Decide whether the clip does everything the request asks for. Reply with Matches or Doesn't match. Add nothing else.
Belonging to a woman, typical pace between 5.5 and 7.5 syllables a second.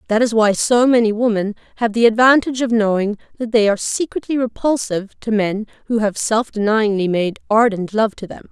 Matches